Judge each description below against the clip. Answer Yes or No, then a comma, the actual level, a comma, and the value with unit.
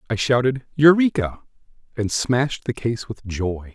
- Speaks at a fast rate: No, average, 145 wpm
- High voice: No, low, 120 Hz